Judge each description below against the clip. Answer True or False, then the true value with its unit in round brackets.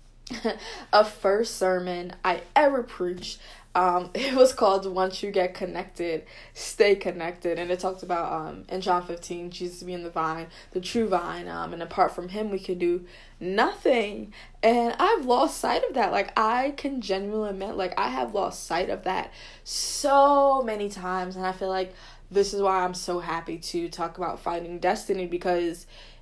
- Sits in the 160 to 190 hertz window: True (185 Hz)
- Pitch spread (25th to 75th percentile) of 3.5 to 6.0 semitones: False (2.5 semitones)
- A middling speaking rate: True (175 wpm)